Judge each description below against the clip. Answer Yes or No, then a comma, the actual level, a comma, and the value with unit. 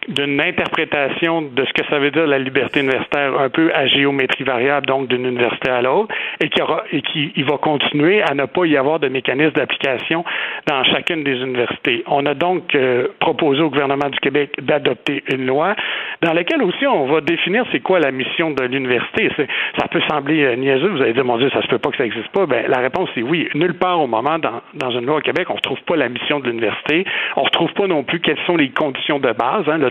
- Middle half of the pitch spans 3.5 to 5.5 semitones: No, narrow, 2.6 semitones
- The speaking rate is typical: No, fast, 240 wpm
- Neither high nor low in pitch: Yes, medium, 145 Hz